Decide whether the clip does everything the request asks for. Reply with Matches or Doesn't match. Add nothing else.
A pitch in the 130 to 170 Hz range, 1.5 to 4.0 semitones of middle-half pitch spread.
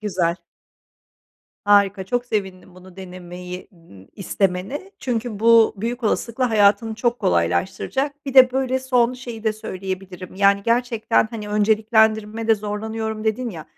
Doesn't match